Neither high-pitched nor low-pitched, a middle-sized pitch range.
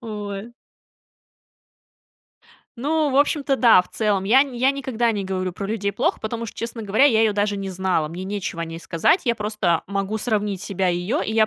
No: high, 210 Hz; average, 3.6 semitones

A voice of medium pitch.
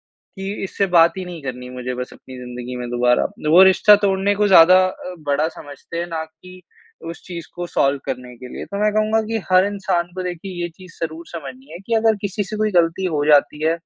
Yes: medium, 170 Hz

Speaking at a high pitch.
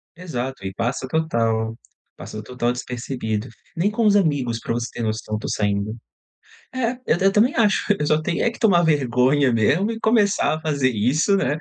No: low, 135 Hz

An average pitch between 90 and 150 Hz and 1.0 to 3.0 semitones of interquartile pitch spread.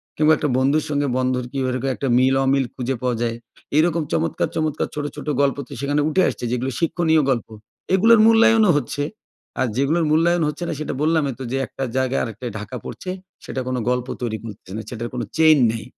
No: medium, 140 Hz; average, 3.9 semitones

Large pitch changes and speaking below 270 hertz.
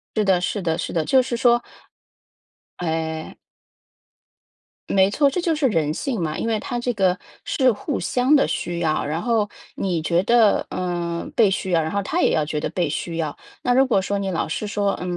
Yes: wide, 6.1 semitones; high, 190 Hz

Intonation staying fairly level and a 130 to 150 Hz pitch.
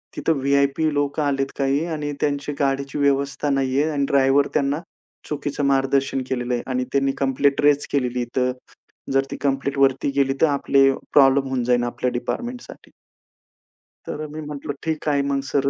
Yes: narrow, 1.2 semitones; medium, 140 Hz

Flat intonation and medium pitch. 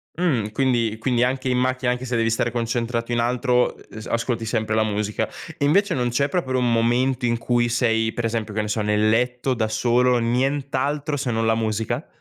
No: narrow, 2.2 semitones; low, 120 Hz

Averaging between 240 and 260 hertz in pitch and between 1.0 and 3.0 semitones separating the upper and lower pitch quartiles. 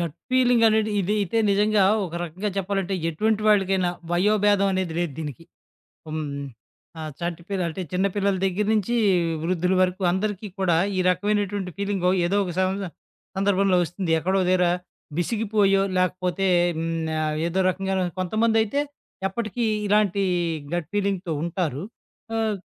No: high, 190 Hz; narrow, 2.6 semitones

